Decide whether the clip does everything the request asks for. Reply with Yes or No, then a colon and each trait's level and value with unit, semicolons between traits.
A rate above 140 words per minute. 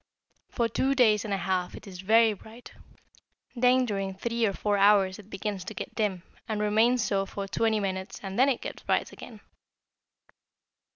Yes: average, 180 wpm